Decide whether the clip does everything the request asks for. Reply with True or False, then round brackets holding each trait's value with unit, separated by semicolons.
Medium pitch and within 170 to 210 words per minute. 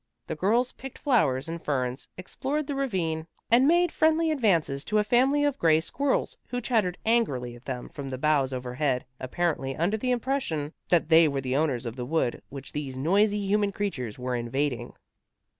True (165 Hz; 180 wpm)